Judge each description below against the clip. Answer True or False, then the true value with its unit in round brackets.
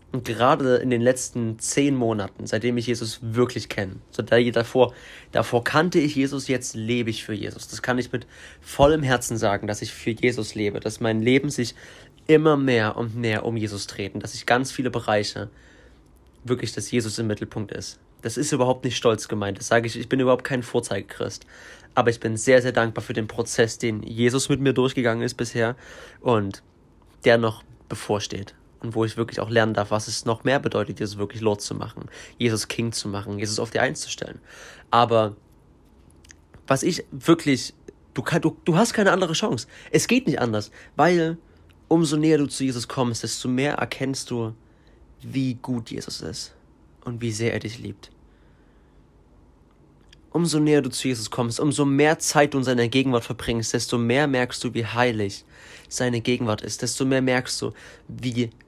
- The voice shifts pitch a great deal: False (2.8 semitones)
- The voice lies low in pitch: True (120 Hz)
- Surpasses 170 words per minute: True (185 wpm)